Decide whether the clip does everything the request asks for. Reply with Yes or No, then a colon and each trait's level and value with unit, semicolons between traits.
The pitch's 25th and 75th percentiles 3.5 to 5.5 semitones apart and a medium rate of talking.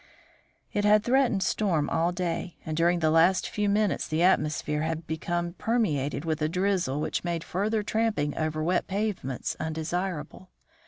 Yes: average, 4.2 semitones; average, 155 wpm